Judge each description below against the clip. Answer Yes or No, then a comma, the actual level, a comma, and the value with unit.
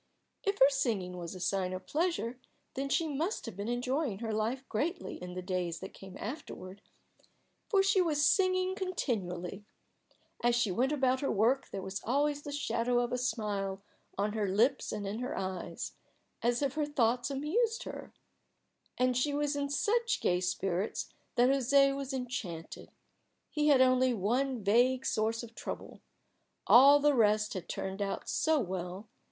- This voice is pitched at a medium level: No, high, 245 Hz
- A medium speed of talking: Yes, average, 170 wpm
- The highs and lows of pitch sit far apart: Yes, wide, 6.1 semitones